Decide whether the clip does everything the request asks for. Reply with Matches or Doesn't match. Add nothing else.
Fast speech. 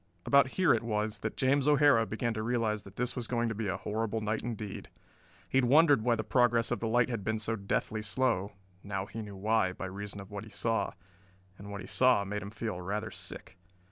Matches